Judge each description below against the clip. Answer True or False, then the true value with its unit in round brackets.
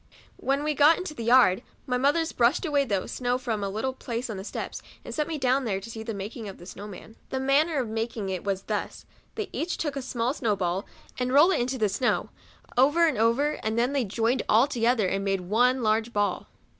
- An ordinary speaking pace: False (255 wpm)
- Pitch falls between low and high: False (240 Hz)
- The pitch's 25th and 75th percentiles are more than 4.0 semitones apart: True (4.4 semitones)